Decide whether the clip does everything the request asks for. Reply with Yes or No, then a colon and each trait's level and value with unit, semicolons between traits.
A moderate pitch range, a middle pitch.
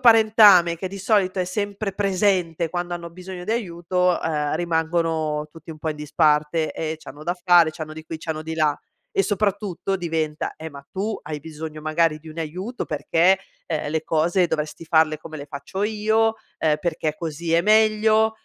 Yes: average, 3.6 semitones; medium, 170 Hz